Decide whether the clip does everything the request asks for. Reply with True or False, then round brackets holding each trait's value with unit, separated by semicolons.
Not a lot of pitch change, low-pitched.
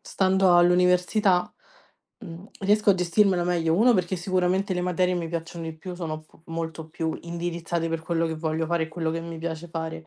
False (1.9 semitones; 170 Hz)